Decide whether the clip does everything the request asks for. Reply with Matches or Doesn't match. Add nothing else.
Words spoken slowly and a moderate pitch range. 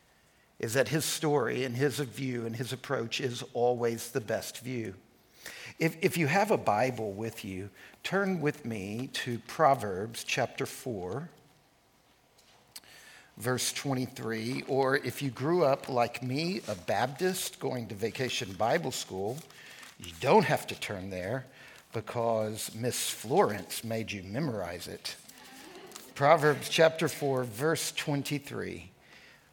Matches